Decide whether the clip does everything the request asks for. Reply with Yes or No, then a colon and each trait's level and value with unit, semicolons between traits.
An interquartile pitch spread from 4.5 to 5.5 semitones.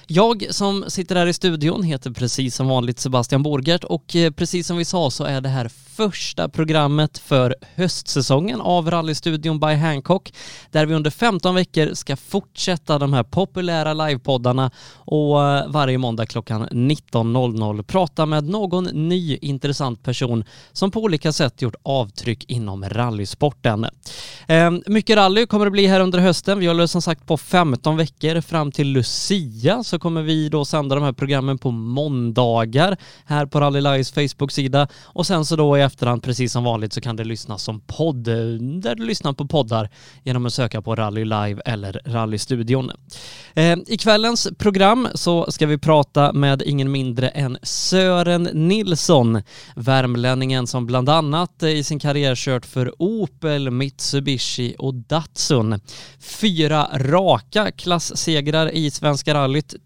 Yes: average, 4.9 semitones